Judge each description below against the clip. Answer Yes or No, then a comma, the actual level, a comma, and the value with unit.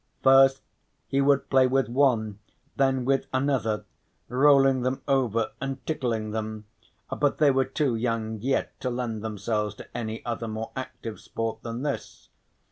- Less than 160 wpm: Yes, average, 150 wpm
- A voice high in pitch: No, low, 125 Hz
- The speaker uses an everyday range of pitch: Yes, average, 3.3 semitones